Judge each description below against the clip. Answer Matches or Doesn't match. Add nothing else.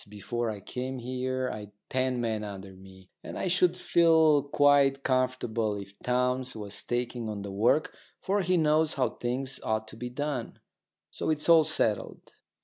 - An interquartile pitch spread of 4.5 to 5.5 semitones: Matches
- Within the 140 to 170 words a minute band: Matches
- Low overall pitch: Matches